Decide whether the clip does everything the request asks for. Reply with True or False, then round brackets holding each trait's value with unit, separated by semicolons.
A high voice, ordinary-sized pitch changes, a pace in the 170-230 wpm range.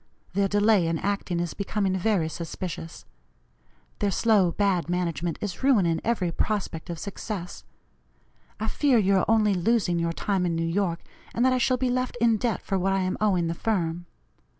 True (195 Hz; 3.9 semitones; 180 wpm)